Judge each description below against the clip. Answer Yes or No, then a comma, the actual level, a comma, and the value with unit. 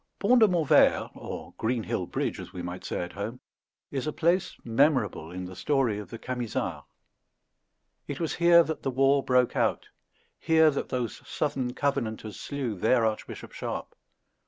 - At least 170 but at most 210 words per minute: No, average, 160 wpm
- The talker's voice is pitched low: Yes, low, 130 Hz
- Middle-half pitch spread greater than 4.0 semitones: Yes, wide, 5.4 semitones